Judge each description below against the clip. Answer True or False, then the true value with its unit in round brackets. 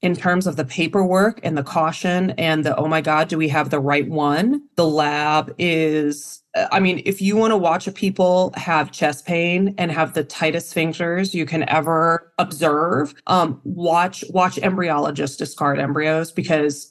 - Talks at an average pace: True (175 wpm)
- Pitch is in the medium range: True (165 Hz)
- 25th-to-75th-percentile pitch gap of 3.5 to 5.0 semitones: False (2.8 semitones)